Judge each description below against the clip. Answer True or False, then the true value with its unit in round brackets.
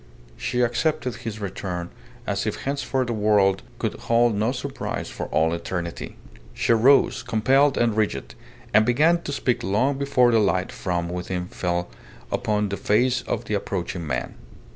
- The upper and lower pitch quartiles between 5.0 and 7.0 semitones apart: True (5.5 semitones)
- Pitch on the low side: True (110 Hz)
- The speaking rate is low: False (160 wpm)